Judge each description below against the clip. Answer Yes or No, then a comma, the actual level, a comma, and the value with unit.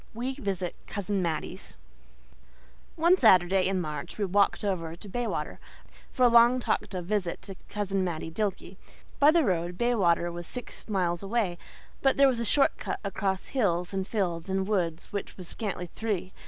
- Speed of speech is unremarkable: Yes, average, 170 wpm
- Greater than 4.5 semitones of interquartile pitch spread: No, average, 4.2 semitones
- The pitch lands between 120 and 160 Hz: No, high, 195 Hz